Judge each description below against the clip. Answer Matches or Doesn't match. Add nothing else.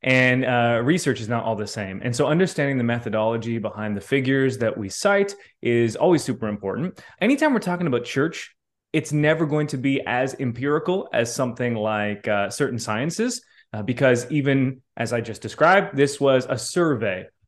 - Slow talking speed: Doesn't match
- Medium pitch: Doesn't match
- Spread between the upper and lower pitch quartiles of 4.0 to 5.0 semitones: Matches